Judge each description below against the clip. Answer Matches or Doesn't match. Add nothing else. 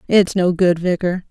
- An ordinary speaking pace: Matches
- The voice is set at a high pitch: Doesn't match